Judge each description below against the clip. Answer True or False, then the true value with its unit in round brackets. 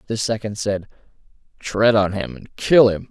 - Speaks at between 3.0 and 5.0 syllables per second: True (4.6 syllables/s)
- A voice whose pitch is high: False (105 Hz)